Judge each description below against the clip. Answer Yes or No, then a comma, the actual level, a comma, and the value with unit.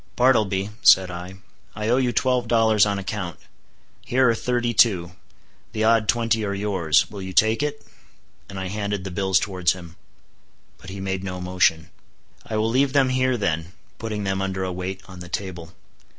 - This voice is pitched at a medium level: No, low, 100 Hz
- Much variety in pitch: No, average, 3.5 semitones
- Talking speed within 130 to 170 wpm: No, average, 180 wpm